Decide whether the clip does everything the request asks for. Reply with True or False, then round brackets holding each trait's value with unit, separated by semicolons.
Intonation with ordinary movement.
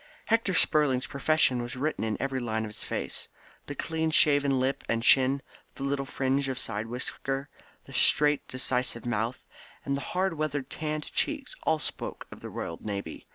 True (3.2 semitones)